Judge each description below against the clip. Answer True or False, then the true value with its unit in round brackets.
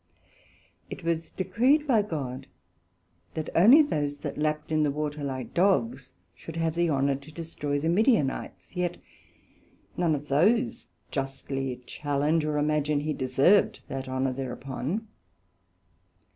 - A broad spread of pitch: False (4.0 semitones)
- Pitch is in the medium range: True (150 Hz)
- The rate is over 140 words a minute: False (135 wpm)